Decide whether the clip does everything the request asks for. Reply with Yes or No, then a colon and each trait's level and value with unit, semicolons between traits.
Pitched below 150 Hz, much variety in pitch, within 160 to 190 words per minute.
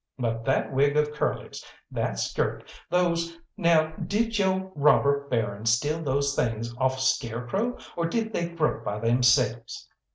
No: medium, 140 Hz; wide, 5.8 semitones; average, 150 wpm